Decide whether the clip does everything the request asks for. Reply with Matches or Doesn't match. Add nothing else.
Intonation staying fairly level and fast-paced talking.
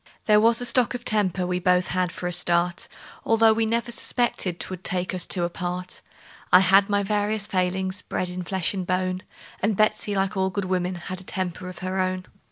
Matches